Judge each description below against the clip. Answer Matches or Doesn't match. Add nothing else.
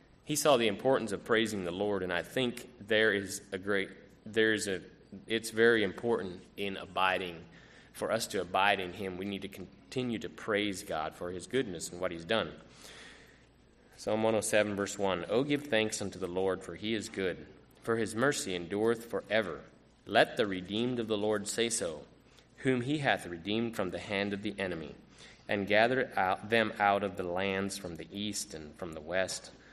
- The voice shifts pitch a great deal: Doesn't match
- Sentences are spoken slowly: Doesn't match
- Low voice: Matches